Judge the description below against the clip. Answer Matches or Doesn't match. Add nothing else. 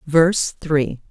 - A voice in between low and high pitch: Matches